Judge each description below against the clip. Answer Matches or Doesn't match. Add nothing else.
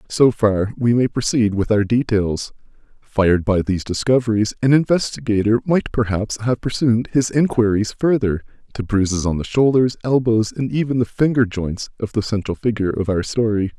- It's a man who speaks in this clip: Matches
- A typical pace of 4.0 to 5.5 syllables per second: Matches